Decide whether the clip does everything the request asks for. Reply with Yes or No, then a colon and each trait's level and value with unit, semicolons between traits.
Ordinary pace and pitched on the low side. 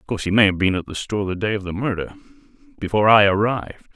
No: fast, 245 wpm; low, 105 Hz